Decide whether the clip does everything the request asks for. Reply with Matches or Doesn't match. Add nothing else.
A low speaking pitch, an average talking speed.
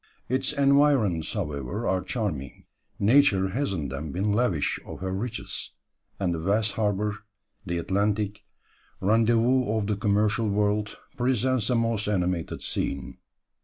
Doesn't match